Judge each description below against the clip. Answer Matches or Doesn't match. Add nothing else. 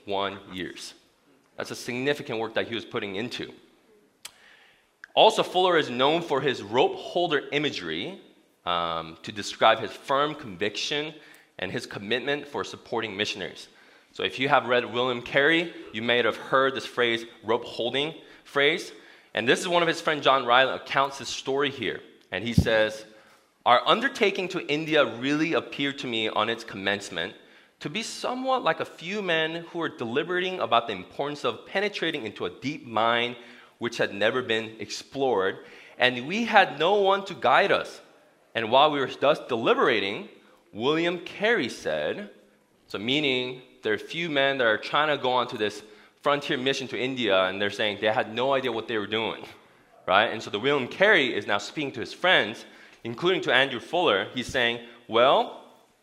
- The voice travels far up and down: Matches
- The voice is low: Matches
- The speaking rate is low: Doesn't match